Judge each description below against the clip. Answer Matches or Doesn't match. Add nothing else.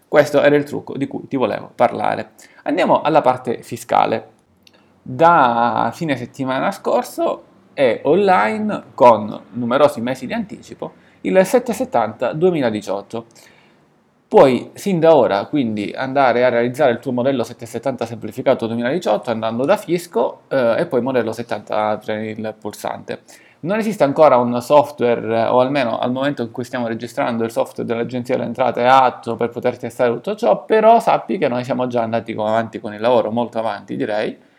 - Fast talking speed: Doesn't match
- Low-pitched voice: Matches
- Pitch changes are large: Doesn't match